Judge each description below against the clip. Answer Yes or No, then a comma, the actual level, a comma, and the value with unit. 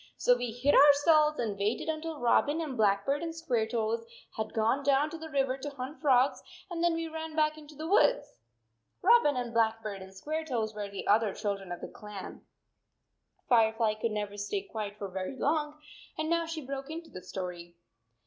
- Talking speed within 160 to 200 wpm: Yes, average, 185 wpm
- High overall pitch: Yes, very high, 255 Hz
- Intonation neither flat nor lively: No, wide, 6.4 semitones